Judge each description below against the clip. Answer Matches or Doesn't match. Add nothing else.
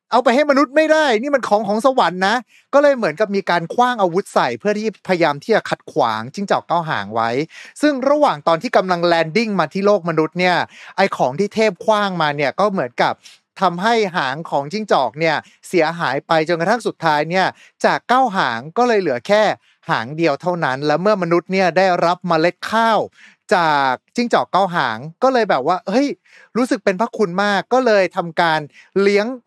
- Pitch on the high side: Matches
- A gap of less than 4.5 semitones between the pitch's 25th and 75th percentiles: Doesn't match